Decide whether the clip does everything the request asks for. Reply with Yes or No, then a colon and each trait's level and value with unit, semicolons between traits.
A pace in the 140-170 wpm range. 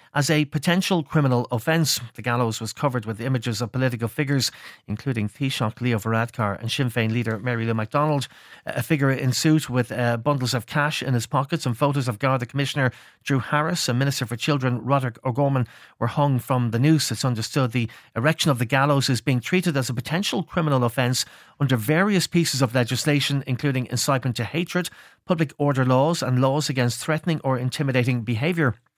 No: average, 185 wpm